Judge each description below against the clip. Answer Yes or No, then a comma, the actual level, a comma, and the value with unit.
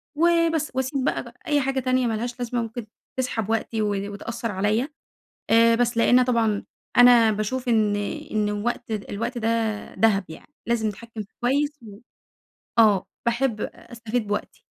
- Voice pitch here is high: Yes, high, 230 Hz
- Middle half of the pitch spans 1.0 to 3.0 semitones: Yes, average, 2.7 semitones